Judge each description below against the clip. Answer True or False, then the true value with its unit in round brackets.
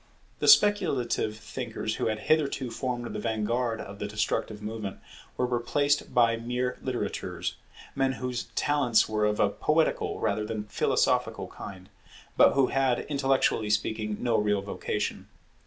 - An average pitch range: True (3.5 semitones)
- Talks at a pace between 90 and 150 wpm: True (140 wpm)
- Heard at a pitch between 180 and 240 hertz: False (115 Hz)